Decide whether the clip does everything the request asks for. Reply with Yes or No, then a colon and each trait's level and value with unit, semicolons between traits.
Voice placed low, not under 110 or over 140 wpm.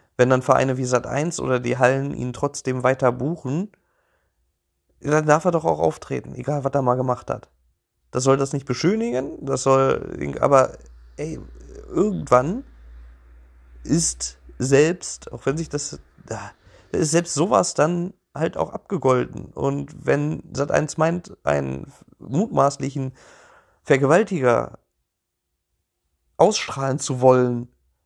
Yes: low, 130 Hz; slow, 125 wpm